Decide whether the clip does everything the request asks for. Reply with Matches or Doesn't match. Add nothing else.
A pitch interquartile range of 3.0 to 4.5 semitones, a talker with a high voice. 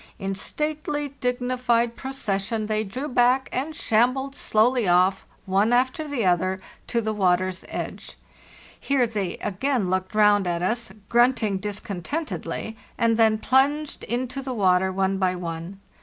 Doesn't match